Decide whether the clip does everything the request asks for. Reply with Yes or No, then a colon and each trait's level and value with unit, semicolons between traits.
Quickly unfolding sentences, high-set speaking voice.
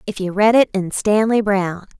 Yes: fast, 210 wpm; high, 200 Hz